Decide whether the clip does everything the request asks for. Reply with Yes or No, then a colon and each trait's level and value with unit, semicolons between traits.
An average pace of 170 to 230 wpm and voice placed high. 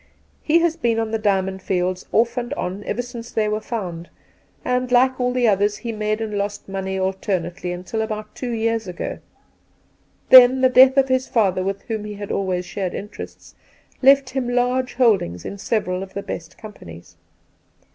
Yes: average, 175 wpm; high, 215 Hz